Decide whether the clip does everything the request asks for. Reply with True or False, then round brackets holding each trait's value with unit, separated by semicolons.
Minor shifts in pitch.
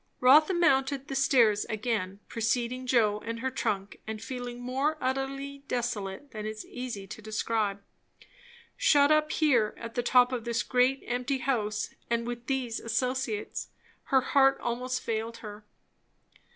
False (3.3 semitones)